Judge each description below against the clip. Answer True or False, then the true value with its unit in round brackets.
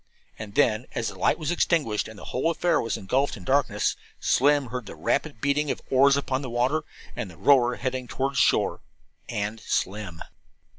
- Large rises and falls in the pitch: False (4.6 semitones)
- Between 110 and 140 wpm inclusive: False (190 wpm)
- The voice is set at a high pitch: False (125 Hz)